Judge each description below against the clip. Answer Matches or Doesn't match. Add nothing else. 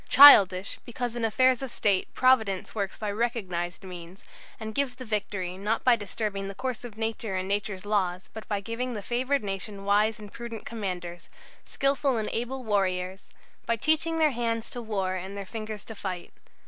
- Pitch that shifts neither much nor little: Matches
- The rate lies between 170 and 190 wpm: Matches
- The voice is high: Matches